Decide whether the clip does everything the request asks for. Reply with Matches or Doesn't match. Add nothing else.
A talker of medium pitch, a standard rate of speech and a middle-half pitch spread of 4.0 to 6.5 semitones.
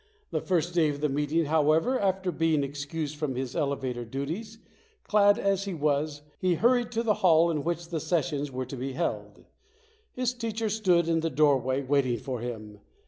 Matches